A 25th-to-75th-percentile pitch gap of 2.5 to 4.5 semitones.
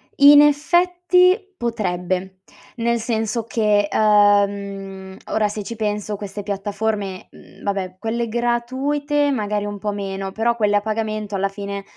Yes: average, 2.9 semitones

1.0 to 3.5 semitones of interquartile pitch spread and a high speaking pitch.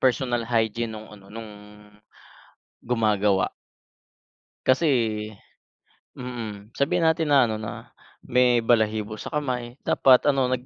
No: average, 2.9 semitones; low, 120 Hz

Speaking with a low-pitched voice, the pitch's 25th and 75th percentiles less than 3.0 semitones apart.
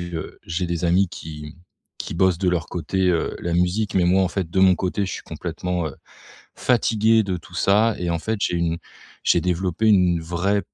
Yes: very low, 90 Hz; narrow, 2.4 semitones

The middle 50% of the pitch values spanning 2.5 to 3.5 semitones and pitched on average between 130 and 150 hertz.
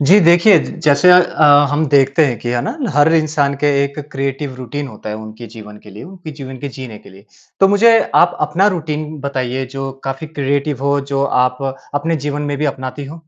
Yes: average, 3.2 semitones; medium, 140 Hz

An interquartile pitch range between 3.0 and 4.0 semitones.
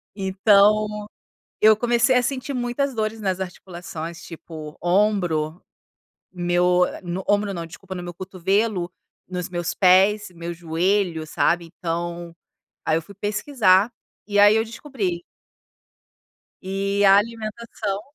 Yes: average, 3.4 semitones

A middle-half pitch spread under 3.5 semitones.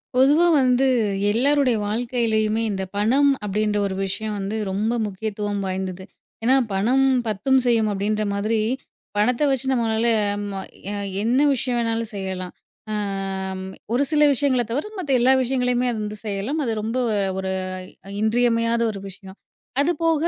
No: average, 3.8 semitones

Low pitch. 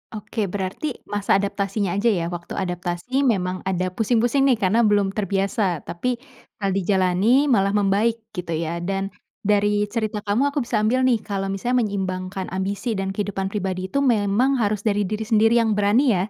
No: high, 205 Hz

